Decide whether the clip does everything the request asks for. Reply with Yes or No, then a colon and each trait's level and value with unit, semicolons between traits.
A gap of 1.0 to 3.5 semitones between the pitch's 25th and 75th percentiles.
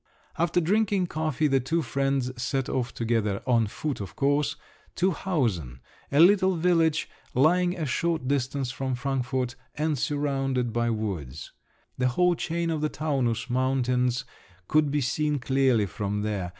No: average, 4.3 semitones